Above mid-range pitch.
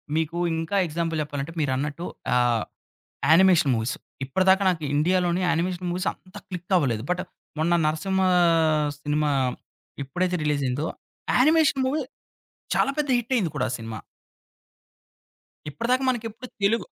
No: medium, 175 Hz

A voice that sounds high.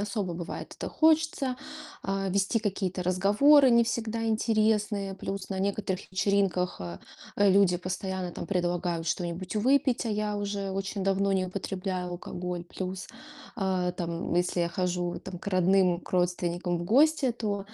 Yes: high, 195 Hz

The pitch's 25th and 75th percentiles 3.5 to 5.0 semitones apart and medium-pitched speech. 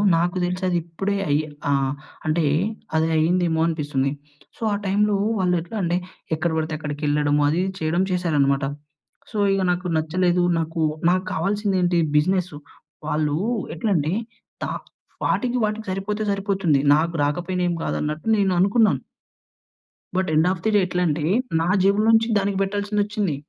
Yes: average, 3.8 semitones; medium, 175 Hz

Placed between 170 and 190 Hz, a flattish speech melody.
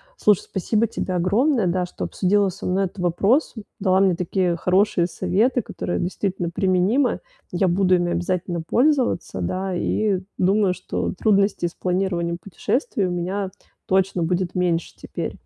Yes: medium, 185 Hz; narrow, 2.2 semitones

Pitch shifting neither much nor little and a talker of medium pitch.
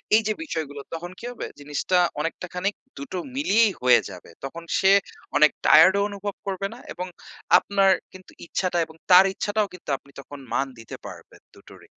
Yes: average, 4.7 semitones; medium, 180 Hz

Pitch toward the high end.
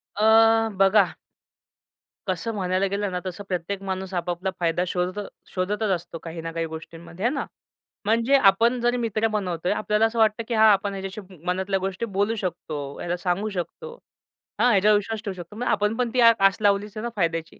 Yes: high, 195 Hz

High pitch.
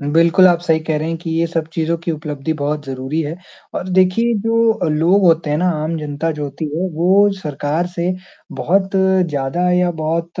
No: medium, 165 Hz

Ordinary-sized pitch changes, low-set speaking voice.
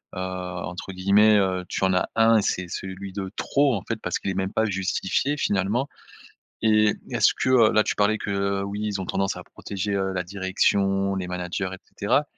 No: narrow, 2.1 semitones; low, 100 Hz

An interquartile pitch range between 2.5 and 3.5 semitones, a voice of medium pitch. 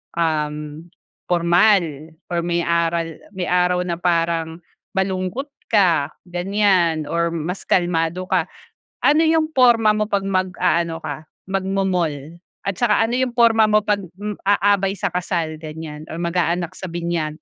Yes: average, 3.1 semitones; medium, 175 Hz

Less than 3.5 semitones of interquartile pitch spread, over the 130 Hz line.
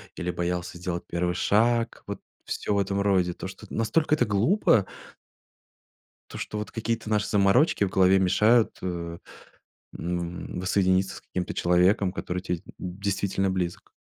No: average, 3.0 semitones; very low, 95 Hz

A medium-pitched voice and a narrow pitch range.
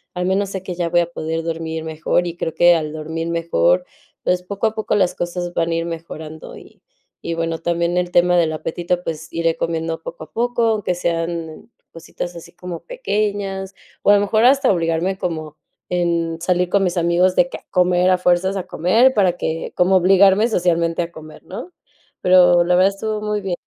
Yes: medium, 175 Hz; narrow, 2.3 semitones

